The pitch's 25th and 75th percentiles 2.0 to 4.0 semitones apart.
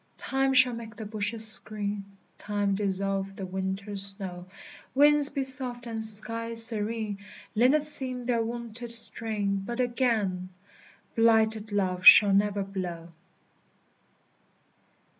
Yes: average, 3.1 semitones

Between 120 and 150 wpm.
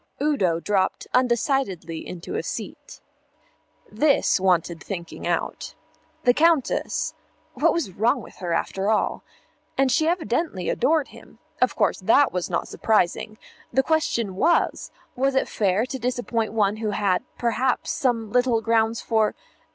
Yes: average, 140 wpm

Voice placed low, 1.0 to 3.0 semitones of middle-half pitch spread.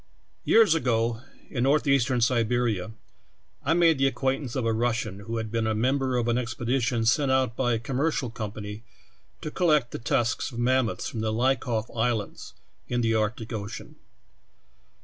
Yes: low, 120 Hz; average, 2.7 semitones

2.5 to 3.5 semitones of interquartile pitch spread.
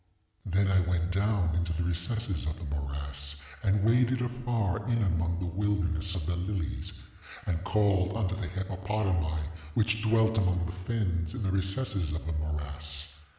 No: average, 3.9 semitones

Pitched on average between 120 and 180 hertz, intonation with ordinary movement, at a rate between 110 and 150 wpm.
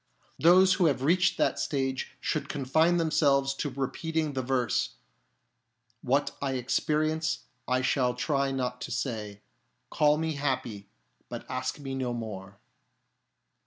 Yes: low, 135 Hz; average, 3.7 semitones; slow, 135 wpm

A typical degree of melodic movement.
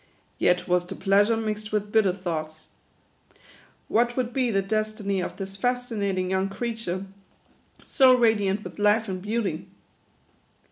Yes: average, 3.0 semitones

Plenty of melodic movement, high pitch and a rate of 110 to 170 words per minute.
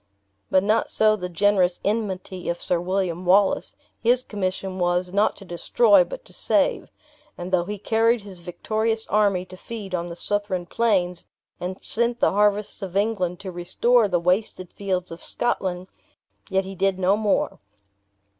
No: average, 2.9 semitones; high, 195 Hz; average, 165 wpm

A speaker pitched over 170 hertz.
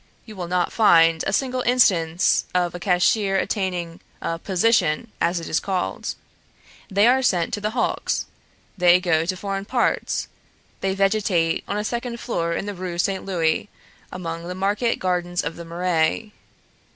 Yes: medium, 185 Hz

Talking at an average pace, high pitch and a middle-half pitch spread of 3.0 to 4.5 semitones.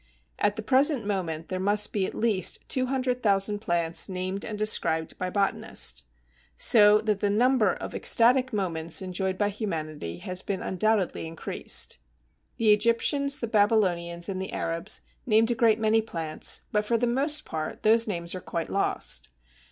Yes: average, 160 wpm; high, 205 Hz; average, 3.8 semitones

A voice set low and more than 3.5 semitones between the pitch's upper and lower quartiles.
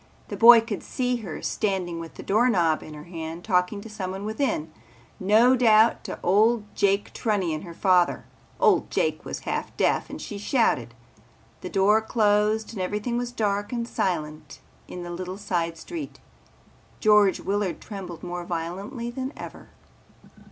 No: high, 200 Hz; average, 4.0 semitones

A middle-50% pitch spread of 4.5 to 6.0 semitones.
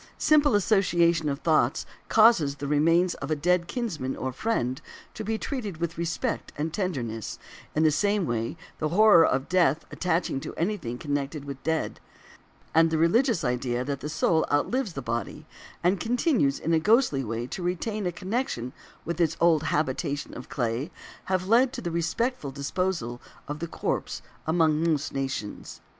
Yes: average, 5.2 semitones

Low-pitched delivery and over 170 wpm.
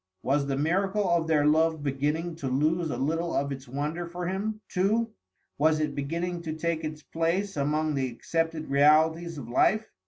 No: medium, 160 Hz; average, 180 wpm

